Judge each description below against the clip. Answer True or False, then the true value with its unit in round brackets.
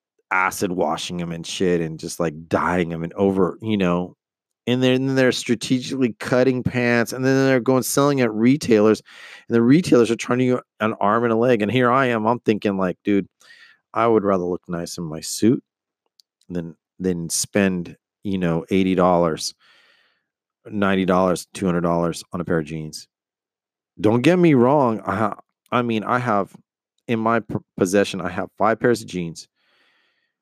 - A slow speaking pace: False (185 wpm)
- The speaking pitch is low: True (105 Hz)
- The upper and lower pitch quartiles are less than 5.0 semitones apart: False (5.6 semitones)